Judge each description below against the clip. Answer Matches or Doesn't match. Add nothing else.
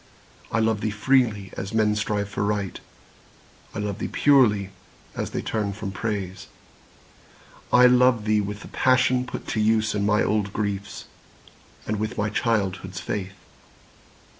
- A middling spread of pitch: Doesn't match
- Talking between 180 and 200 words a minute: Doesn't match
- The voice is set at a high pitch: Doesn't match